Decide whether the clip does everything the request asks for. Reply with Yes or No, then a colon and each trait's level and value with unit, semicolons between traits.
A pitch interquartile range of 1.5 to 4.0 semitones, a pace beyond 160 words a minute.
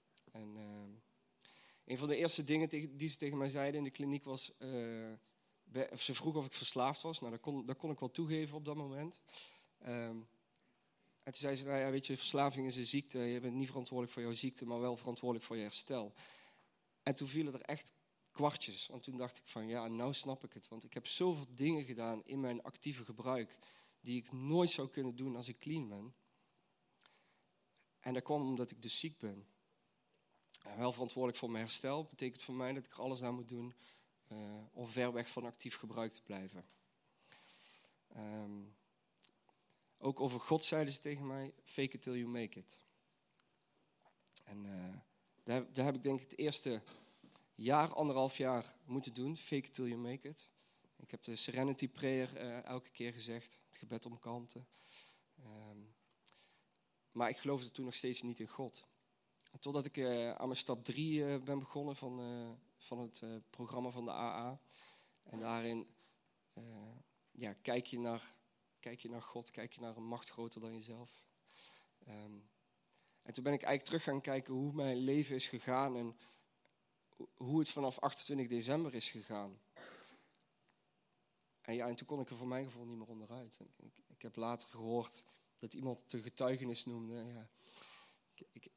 Yes: average, 2.8 semitones; average, 185 wpm